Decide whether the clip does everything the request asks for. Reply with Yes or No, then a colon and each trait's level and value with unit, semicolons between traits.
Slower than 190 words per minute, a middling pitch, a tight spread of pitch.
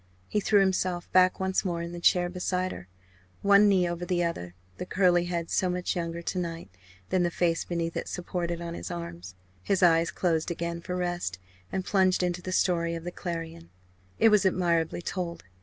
No: average, 195 wpm; medium, 175 Hz; narrow, 1.5 semitones